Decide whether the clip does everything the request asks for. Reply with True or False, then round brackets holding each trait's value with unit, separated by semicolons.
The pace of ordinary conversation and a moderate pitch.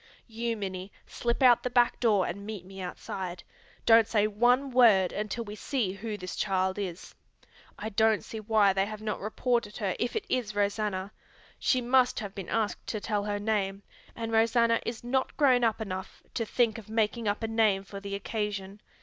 False (190 wpm; 215 Hz)